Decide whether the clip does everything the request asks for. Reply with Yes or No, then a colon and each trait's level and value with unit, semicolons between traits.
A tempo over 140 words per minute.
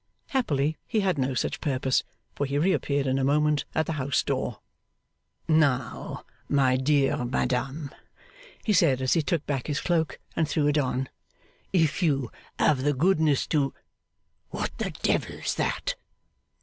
Yes: average, 150 wpm